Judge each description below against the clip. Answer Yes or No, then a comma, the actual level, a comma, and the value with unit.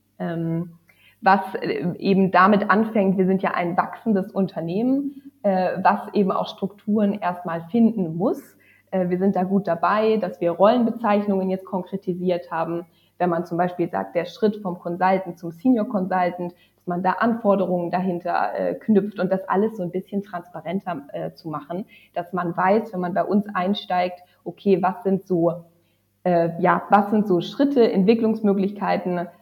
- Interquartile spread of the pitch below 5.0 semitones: Yes, narrow, 2.5 semitones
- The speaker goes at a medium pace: Yes, average, 160 wpm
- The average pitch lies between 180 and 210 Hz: Yes, medium, 185 Hz